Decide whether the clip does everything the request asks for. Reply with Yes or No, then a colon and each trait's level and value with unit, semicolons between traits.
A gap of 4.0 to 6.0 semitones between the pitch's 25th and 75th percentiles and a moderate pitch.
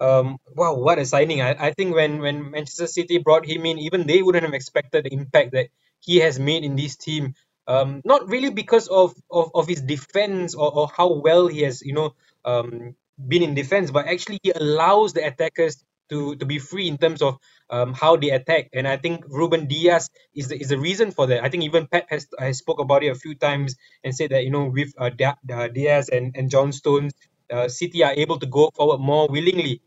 No: average, 3.6 semitones; medium, 150 Hz